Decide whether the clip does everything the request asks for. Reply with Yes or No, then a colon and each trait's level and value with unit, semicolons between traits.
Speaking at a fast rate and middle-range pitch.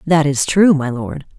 Yes: fast, 215 wpm; medium, 150 Hz